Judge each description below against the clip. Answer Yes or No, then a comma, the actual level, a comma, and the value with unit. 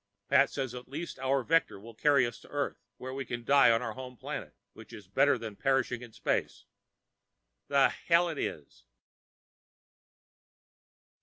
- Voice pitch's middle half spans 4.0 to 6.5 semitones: No, average, 3.0 semitones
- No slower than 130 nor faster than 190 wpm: Yes, average, 160 wpm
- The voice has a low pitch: Yes, low, 130 Hz